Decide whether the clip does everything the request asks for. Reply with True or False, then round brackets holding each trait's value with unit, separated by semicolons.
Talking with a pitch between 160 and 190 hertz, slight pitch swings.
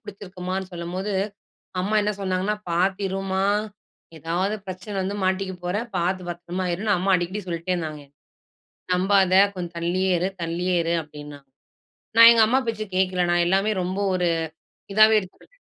True (185 Hz; 2.0 semitones)